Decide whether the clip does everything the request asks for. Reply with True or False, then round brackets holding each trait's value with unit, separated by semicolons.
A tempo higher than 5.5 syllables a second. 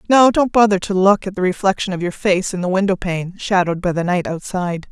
True (6.0 syllables/s)